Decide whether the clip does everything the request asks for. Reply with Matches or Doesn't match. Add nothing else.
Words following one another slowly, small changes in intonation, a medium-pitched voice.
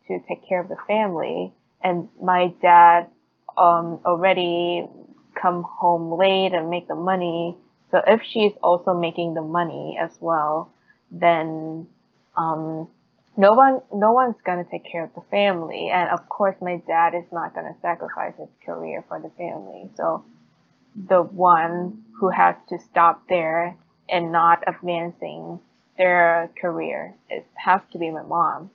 Matches